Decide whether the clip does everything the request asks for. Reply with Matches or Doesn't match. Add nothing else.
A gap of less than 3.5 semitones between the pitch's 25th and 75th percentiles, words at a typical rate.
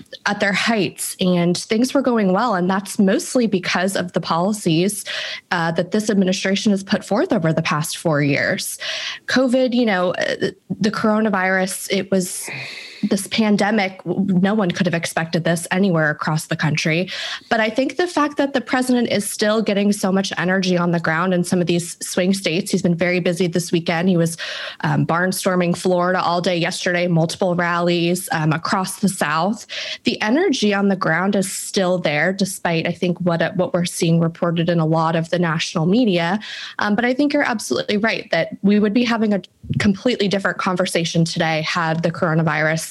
Matches